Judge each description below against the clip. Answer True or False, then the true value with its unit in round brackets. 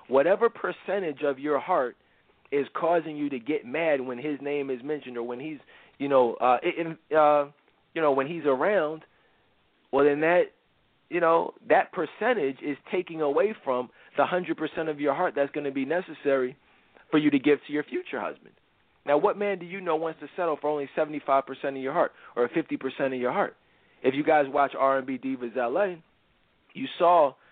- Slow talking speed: False (195 wpm)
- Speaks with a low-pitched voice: False (145 Hz)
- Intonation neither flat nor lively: True (3.2 semitones)